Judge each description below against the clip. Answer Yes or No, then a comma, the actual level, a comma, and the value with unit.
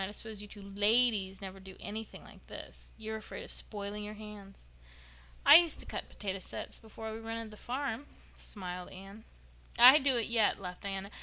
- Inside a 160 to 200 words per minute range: Yes, average, 190 wpm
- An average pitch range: No, narrow, 2.3 semitones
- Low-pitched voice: No, high, 210 Hz